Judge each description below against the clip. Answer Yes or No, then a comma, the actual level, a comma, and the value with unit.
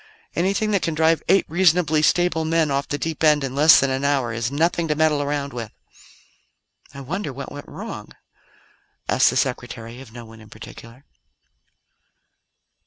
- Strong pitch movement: No, average, 3.5 semitones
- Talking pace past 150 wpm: Yes, average, 170 wpm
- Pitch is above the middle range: No, medium, 145 Hz